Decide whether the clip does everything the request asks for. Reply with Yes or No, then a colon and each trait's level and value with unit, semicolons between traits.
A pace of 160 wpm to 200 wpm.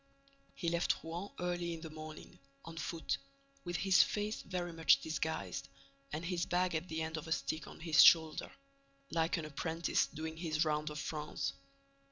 Yes: average, 175 wpm